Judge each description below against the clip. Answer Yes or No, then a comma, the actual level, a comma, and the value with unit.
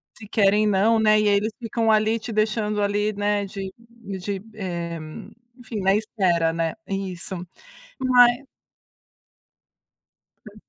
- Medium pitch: No, high, 210 Hz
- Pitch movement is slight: Yes, narrow, 2.1 semitones